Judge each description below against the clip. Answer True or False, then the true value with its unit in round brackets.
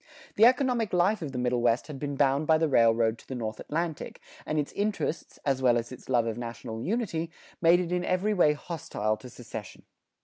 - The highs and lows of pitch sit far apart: True (6.7 semitones)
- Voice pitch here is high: False (145 Hz)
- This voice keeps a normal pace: False (210 wpm)